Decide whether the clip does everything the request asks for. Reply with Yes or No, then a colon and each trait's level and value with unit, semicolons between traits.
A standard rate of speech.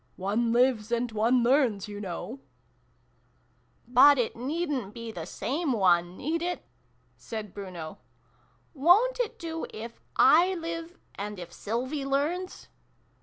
Yes: average, 150 wpm